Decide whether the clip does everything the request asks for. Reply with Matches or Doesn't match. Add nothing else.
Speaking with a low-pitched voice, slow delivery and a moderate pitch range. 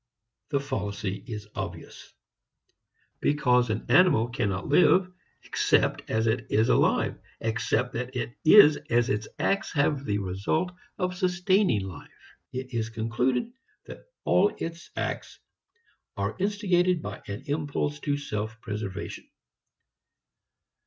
Doesn't match